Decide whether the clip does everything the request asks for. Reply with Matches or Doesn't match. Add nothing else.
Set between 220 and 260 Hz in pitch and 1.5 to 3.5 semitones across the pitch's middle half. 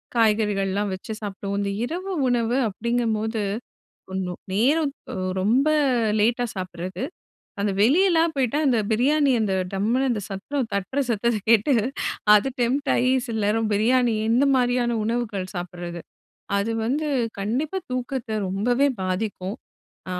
Doesn't match